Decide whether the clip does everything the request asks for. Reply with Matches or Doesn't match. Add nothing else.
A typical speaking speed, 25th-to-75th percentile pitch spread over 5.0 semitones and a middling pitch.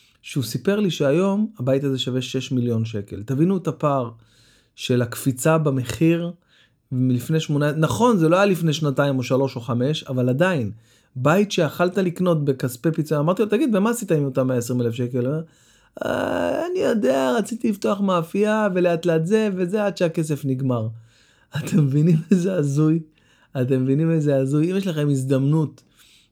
Doesn't match